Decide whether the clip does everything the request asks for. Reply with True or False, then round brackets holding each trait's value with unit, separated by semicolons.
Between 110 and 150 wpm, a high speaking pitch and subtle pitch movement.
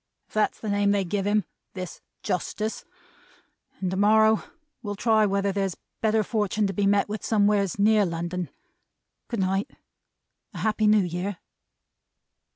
True (145 wpm; 205 Hz; 1.8 semitones)